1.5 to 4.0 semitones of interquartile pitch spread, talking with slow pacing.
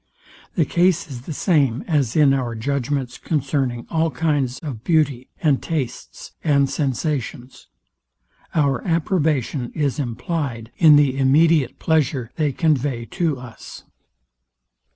Yes: average, 3.6 semitones; slow, 120 wpm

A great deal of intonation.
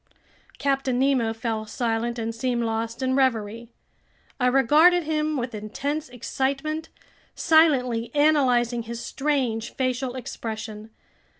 No: average, 3.4 semitones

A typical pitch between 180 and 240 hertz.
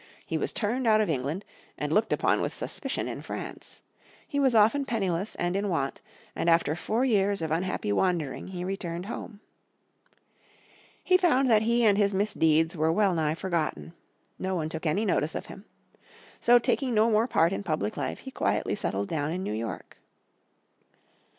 Yes: high, 190 Hz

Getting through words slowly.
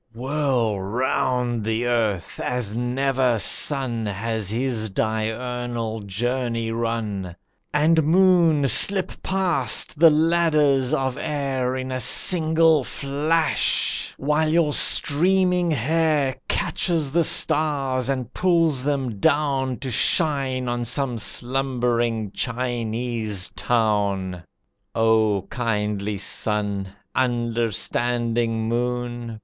Yes: slow, 95 wpm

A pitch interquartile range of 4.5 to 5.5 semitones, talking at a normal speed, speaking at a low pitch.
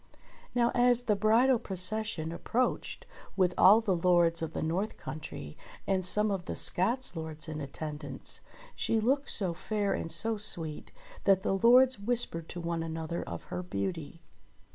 No: average, 5.1 semitones; average, 160 wpm; medium, 185 Hz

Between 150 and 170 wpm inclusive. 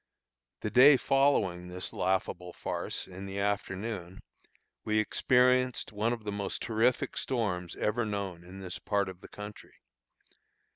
No: average, 140 wpm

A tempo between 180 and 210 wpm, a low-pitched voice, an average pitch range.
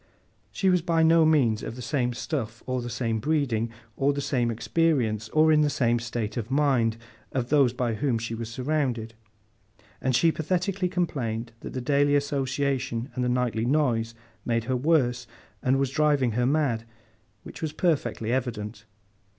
No: average, 165 wpm; low, 130 Hz; average, 4.2 semitones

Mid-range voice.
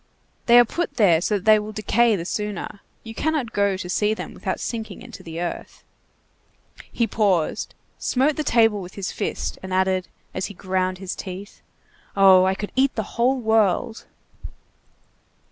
No: high, 205 Hz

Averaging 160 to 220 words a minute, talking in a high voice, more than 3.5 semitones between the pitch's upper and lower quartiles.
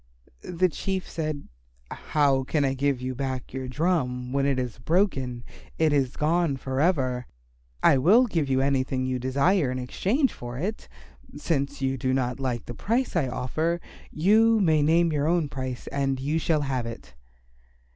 No: average, 170 wpm; medium, 140 Hz; average, 4.3 semitones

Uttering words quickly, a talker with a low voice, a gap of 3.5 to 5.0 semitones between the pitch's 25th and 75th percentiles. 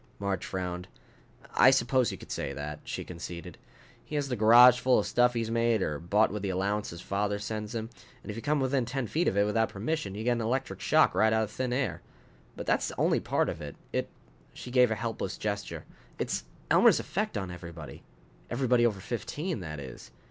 Yes: fast, 215 wpm; low, 110 Hz; average, 4.3 semitones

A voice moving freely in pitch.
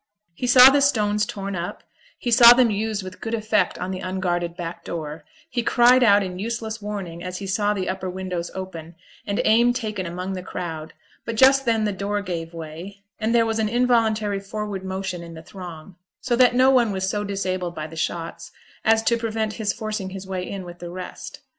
No: average, 3.6 semitones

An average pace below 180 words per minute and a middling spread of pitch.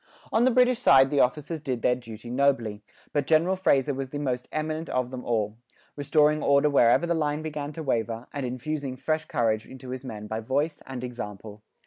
No: average, 195 wpm; average, 3.9 semitones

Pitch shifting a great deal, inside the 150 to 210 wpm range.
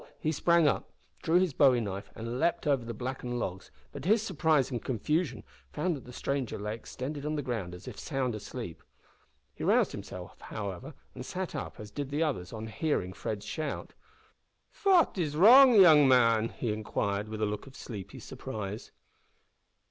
Yes: wide, 6.1 semitones; average, 180 wpm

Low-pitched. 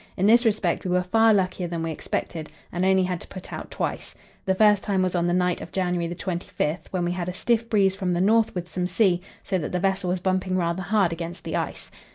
No: medium, 185 Hz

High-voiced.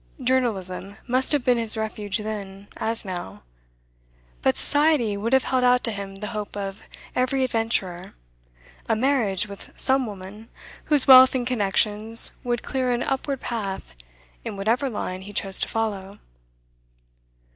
Yes: high, 220 Hz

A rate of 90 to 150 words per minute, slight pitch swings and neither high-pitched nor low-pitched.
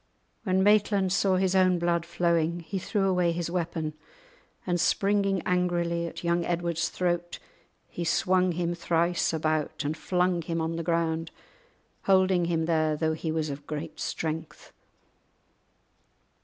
Yes: average, 140 wpm; narrow, 1.9 semitones; medium, 170 Hz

